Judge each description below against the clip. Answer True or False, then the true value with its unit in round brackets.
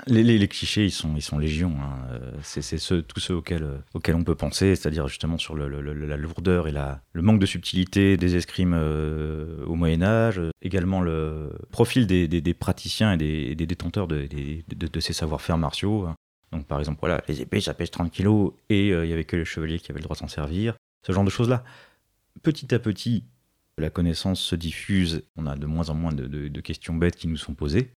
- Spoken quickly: True (235 wpm)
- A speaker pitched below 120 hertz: True (85 Hz)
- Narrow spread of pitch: False (3.7 semitones)